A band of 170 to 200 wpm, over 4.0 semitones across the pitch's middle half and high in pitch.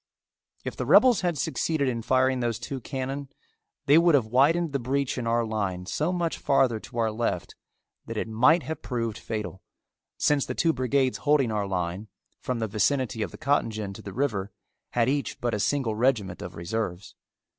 No: average, 190 wpm; average, 4.4 semitones; low, 125 Hz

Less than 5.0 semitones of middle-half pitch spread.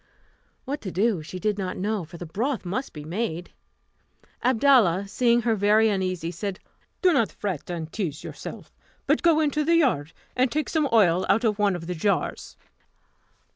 No: wide, 5.5 semitones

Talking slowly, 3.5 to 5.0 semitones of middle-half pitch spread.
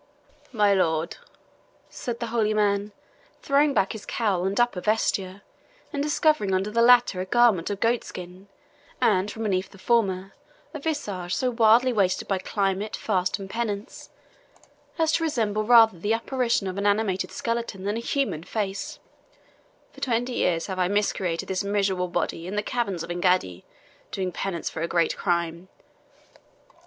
No: average, 160 wpm; average, 3.9 semitones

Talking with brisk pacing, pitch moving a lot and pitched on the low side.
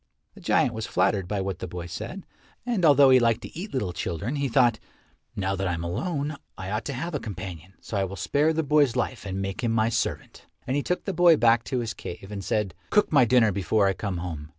Yes: fast, 245 wpm; wide, 6.5 semitones; low, 110 Hz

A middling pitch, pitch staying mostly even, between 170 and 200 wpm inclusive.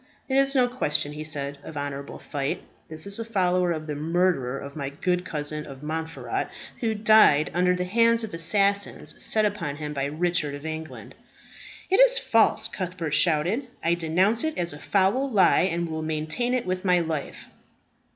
No: medium, 170 Hz; average, 5.3 semitones; average, 180 wpm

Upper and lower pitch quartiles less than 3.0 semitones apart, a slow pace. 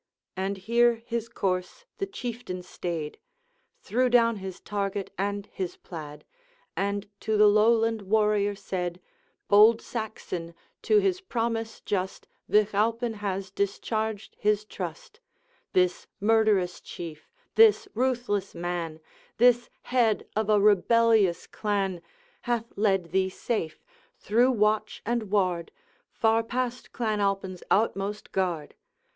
No: average, 3.3 semitones; slow, 120 wpm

